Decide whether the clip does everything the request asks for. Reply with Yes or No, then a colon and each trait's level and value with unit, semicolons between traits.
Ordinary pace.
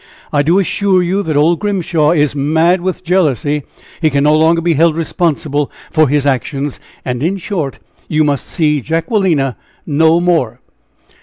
Yes: average, 160 wpm